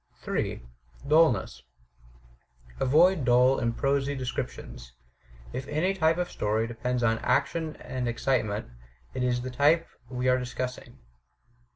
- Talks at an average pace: No, slow, 130 wpm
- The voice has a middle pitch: No, low, 130 Hz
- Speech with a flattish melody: No, average, 3.4 semitones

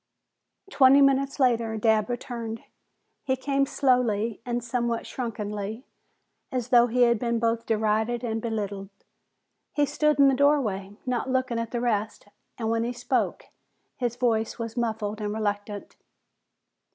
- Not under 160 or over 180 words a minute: No, average, 140 wpm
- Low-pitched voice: No, high, 235 Hz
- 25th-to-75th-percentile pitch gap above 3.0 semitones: No, narrow, 2.5 semitones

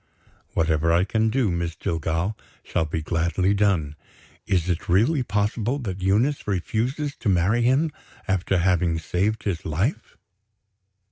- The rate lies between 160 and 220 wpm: No, slow, 135 wpm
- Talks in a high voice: No, very low, 95 Hz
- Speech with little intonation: No, average, 4.6 semitones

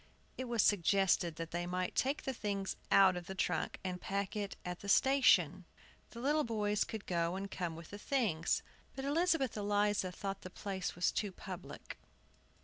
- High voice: Yes, high, 200 Hz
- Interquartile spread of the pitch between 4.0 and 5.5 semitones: No, average, 3.6 semitones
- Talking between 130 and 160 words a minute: No, average, 175 wpm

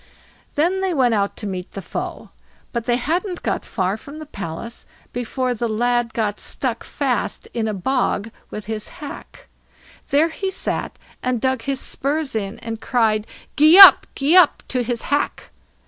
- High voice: Yes, high, 245 Hz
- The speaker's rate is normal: Yes, average, 170 wpm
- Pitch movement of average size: Yes, average, 4.6 semitones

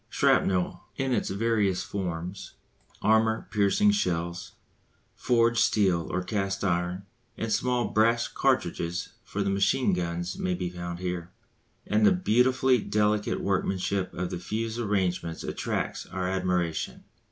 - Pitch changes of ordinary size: Yes, average, 3.8 semitones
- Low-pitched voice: Yes, very low, 95 Hz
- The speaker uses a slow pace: Yes, slow, 130 wpm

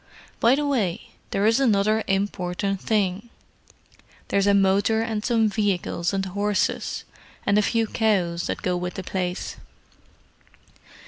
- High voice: Yes, high, 200 Hz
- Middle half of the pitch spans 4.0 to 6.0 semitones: No, average, 2.8 semitones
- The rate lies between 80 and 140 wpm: Yes, slow, 135 wpm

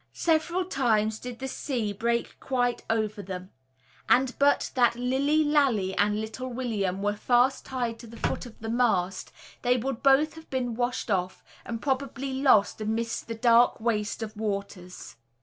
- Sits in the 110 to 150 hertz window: No, high, 235 Hz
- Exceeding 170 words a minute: No, average, 165 wpm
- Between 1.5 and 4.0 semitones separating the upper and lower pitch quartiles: Yes, average, 3.6 semitones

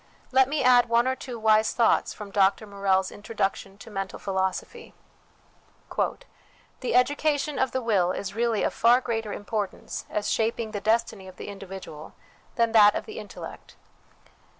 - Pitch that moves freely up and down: No, average, 3.5 semitones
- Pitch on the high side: Yes, high, 220 Hz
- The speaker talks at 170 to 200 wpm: No, average, 160 wpm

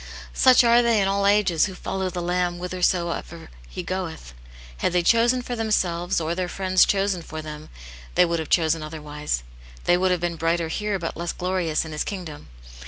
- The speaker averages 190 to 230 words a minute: Yes, average, 200 wpm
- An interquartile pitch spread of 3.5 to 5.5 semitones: No, average, 3.0 semitones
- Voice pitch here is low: No, medium, 175 Hz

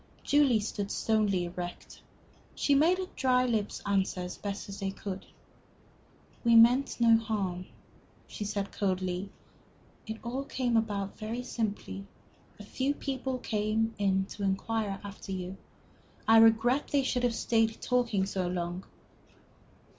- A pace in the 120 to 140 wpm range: Yes, slow, 135 wpm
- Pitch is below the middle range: No, high, 215 Hz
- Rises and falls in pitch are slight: No, average, 3.5 semitones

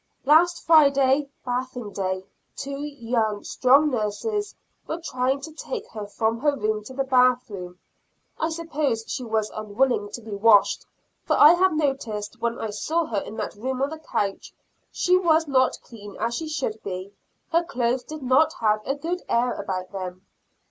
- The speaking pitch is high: Yes, very high, 255 Hz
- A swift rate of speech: No, average, 175 wpm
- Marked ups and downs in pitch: Yes, wide, 5.9 semitones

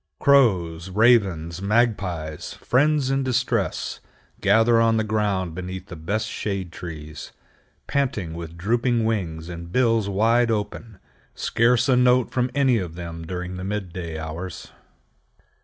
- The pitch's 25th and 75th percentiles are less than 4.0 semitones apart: No, wide, 5.4 semitones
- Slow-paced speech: Yes, slow, 125 wpm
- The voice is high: No, low, 100 Hz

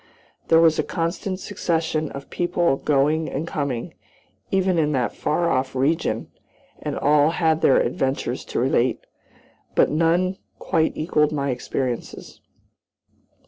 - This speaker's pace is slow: Yes, slow, 130 wpm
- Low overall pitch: No, medium, 155 Hz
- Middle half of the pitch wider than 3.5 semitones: No, average, 3.2 semitones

